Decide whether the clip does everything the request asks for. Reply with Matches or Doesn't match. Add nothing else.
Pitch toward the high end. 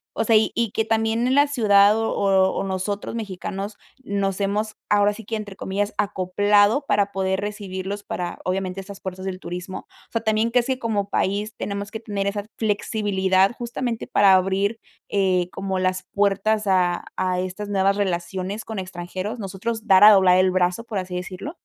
Matches